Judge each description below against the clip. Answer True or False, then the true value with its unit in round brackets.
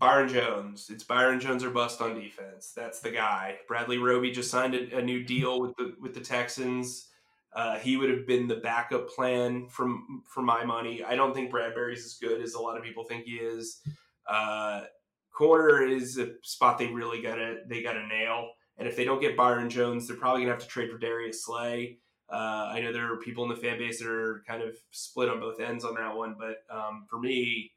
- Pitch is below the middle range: True (120 Hz)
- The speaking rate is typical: False (225 wpm)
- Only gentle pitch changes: True (1.5 semitones)